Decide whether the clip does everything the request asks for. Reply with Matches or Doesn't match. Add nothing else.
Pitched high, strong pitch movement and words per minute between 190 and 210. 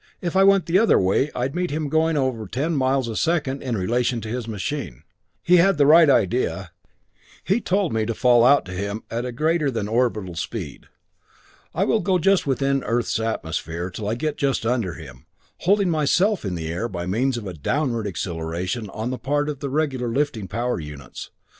Doesn't match